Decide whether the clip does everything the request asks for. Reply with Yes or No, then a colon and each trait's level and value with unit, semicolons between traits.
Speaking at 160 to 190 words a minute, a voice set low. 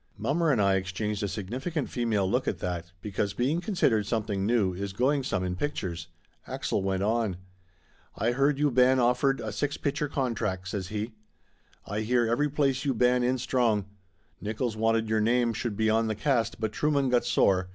Yes: average, 185 wpm; low, 115 Hz